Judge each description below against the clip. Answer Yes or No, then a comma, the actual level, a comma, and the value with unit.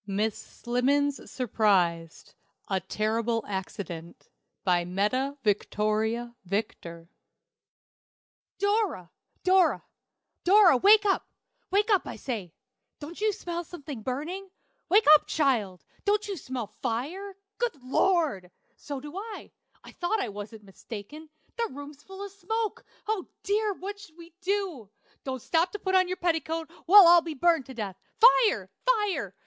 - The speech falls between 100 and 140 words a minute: Yes, slow, 135 wpm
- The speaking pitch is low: No, very high, 295 Hz